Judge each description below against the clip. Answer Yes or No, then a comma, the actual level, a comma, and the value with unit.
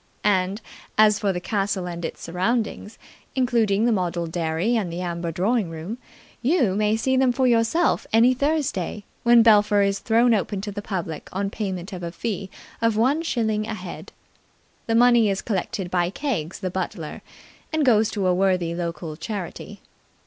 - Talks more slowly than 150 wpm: No, average, 170 wpm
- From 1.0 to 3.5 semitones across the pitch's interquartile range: No, average, 4.2 semitones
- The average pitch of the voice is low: No, high, 205 Hz